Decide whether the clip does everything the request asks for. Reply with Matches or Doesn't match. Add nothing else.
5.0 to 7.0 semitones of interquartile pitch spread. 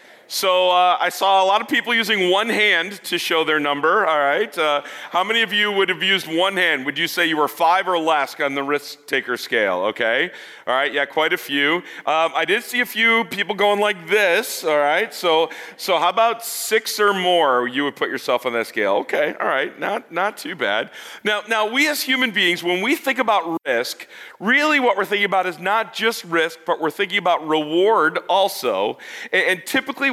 Matches